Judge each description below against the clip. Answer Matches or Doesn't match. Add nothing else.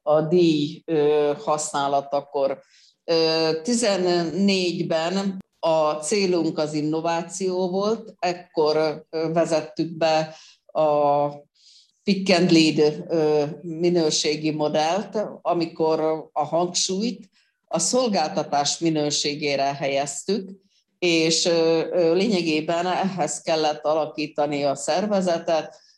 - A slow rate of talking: Matches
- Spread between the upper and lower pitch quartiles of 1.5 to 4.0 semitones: Matches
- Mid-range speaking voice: Matches